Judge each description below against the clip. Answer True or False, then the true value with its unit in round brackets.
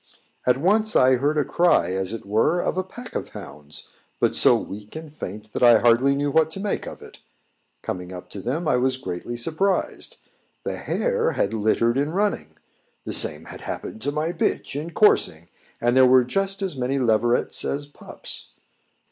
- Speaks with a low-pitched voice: True (130 Hz)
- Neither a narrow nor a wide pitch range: False (7.0 semitones)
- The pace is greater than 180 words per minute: True (190 wpm)